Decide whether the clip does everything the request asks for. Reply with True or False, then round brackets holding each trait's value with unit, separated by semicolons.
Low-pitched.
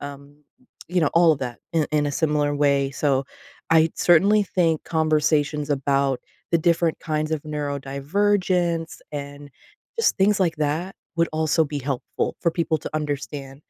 False (150 Hz)